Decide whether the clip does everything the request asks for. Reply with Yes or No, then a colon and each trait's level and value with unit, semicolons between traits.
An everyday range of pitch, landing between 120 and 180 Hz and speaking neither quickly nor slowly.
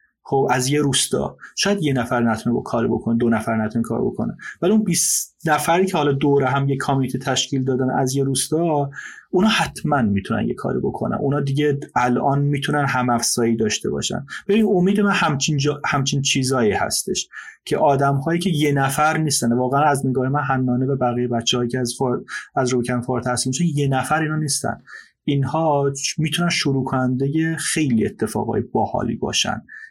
No: average, 3.2 semitones; medium, 140 Hz; fast, 170 wpm